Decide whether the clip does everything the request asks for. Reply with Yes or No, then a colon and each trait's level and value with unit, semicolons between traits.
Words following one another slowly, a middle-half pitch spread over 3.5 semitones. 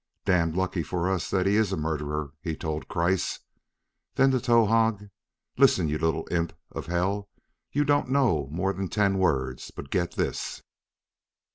No: average, 160 wpm; average, 4.3 semitones